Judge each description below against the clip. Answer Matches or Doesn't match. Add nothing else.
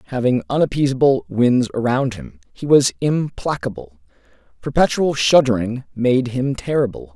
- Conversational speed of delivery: Doesn't match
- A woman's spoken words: Doesn't match